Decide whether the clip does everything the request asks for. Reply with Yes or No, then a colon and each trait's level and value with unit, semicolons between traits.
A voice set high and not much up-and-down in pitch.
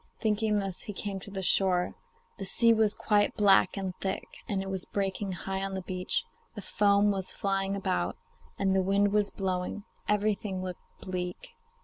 Yes: high, 195 Hz; narrow, 1.5 semitones